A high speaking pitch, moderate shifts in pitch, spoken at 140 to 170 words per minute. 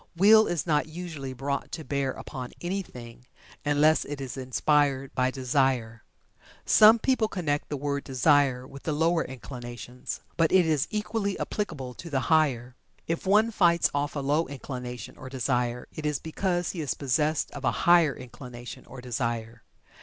No: medium, 140 Hz; average, 4.5 semitones; average, 160 wpm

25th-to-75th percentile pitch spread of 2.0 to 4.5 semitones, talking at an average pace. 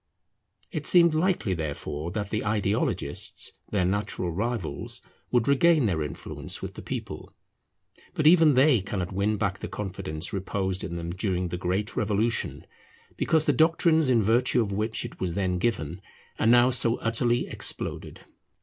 No: average, 5.0 semitones; average, 155 wpm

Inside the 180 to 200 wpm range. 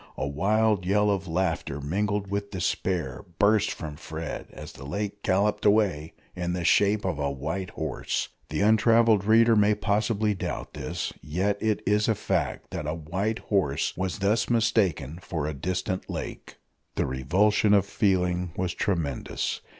No: average, 160 wpm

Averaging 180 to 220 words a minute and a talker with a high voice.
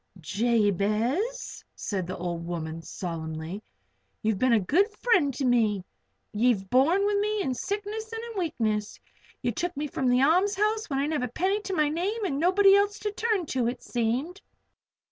Yes: average, 185 wpm; very high, 275 Hz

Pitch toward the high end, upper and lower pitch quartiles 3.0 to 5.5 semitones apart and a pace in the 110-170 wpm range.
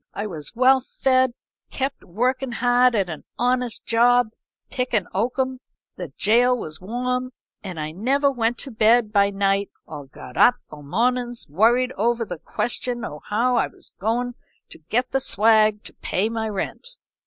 Yes: high, 235 Hz; average, 3.8 semitones; average, 165 wpm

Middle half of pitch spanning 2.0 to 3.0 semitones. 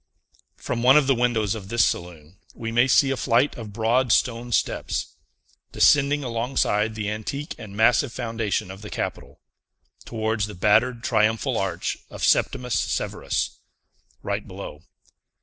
Yes: average, 2.7 semitones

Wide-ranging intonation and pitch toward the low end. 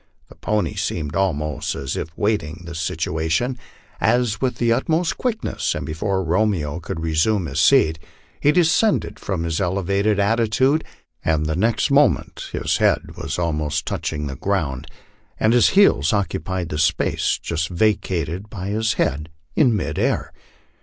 Yes: wide, 5.8 semitones; very low, 95 Hz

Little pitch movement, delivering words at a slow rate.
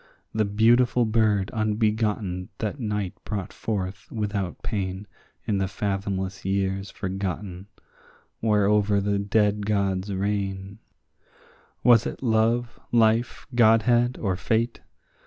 Yes: narrow, 2.3 semitones; slow, 105 wpm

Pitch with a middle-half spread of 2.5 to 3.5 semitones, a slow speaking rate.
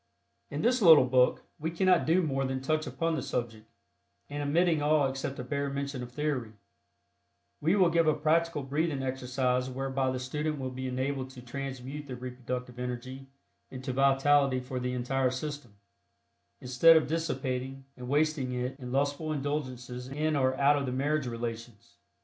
No: average, 2.8 semitones; average, 165 wpm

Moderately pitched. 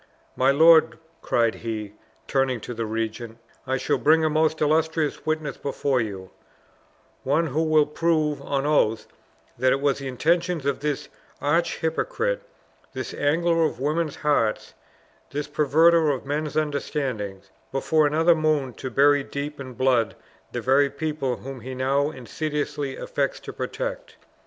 Yes: medium, 145 Hz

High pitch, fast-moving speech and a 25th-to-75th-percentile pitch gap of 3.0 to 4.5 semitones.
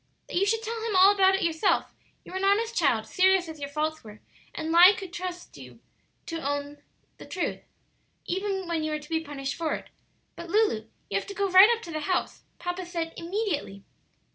Yes: very high, 350 Hz; fast, 215 wpm; average, 3.9 semitones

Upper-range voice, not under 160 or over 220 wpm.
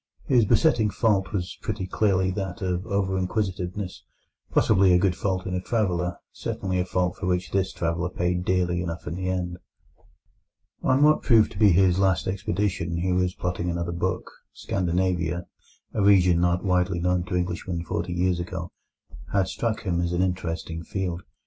No: very low, 90 Hz; average, 170 wpm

